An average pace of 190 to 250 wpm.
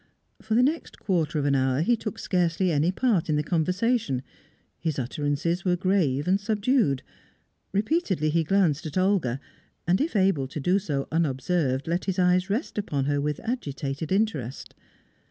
No: average, 165 wpm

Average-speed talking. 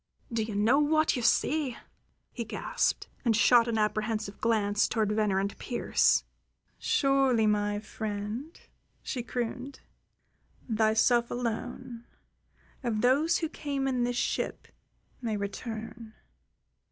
No: slow, 115 wpm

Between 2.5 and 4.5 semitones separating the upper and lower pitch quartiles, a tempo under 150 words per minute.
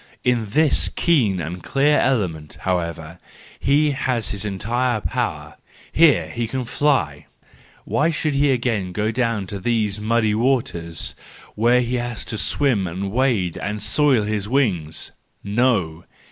No: wide, 5.4 semitones; slow, 135 wpm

